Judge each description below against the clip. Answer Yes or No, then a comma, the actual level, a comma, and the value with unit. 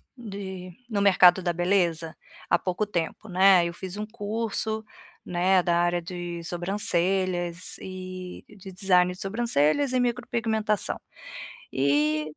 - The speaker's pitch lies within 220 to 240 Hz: No, medium, 185 Hz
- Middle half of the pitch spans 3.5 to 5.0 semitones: No, average, 3.0 semitones